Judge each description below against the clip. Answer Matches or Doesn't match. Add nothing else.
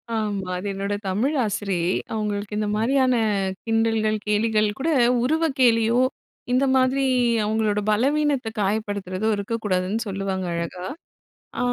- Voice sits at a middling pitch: Doesn't match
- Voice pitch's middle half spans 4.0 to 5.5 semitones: Doesn't match